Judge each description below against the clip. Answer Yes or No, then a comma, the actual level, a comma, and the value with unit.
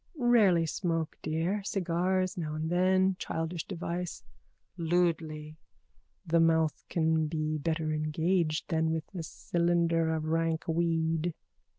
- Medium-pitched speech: Yes, medium, 165 Hz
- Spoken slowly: Yes, slow, 120 wpm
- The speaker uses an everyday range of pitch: No, narrow, 1.7 semitones